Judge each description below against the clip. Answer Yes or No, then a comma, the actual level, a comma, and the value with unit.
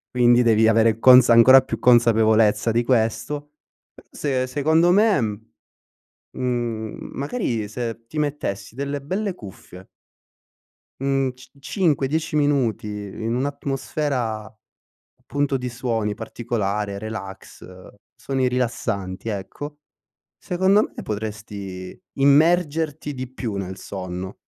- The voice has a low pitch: Yes, low, 120 Hz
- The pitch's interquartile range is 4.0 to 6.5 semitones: Yes, average, 4.7 semitones